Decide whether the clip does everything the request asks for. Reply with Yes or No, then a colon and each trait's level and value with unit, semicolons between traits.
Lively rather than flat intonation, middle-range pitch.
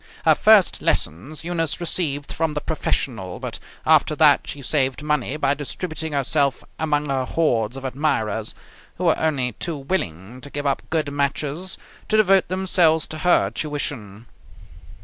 No: average, 3.5 semitones; medium, 145 Hz